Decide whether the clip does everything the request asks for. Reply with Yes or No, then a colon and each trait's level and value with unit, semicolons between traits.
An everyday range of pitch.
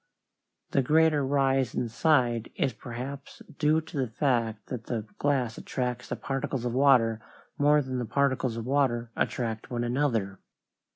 Yes: average, 3.1 semitones